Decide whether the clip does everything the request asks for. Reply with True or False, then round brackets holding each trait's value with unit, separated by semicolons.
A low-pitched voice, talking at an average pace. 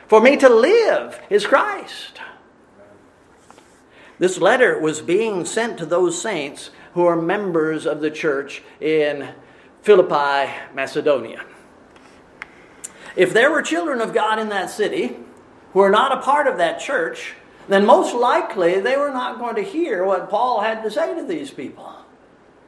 False (205 Hz; 150 wpm)